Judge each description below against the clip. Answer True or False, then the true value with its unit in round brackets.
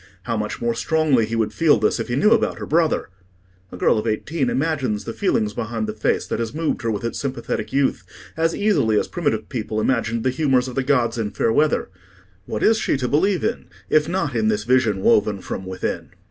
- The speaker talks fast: True (220 wpm)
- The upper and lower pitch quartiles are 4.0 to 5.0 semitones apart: False (5.5 semitones)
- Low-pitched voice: True (120 Hz)